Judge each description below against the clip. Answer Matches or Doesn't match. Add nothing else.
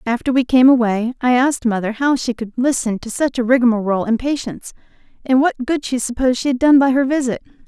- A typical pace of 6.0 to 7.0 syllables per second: Matches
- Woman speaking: Matches